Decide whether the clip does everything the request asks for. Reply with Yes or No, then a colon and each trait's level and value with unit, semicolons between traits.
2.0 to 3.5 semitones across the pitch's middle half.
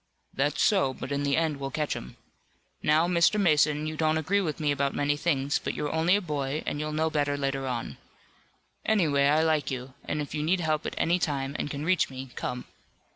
Yes: narrow, 2.4 semitones